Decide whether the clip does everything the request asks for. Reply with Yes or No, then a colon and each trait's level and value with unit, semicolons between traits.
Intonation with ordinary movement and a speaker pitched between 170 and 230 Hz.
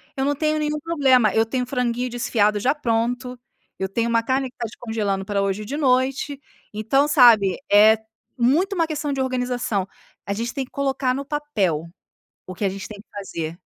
No: average, 4.5 semitones; high, 245 Hz